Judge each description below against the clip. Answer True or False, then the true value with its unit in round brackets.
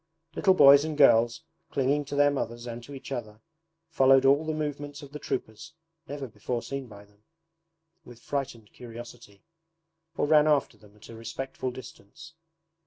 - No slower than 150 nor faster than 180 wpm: True (165 wpm)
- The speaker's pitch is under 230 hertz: True (135 Hz)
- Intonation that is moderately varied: True (3.7 semitones)